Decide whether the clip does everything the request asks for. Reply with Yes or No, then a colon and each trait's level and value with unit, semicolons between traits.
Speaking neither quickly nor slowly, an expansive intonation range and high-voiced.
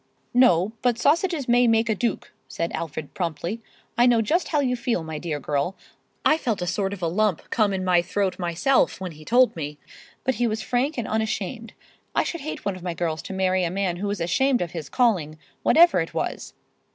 No: fast, 210 wpm; wide, 6.0 semitones; high, 200 Hz